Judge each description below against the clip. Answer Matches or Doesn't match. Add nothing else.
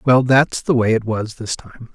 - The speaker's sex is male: Matches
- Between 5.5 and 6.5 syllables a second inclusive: Doesn't match